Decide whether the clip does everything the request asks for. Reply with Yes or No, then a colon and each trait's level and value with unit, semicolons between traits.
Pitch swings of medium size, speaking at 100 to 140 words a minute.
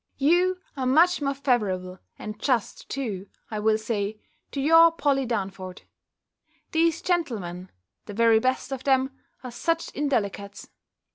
No: wide, 6.0 semitones; slow, 135 wpm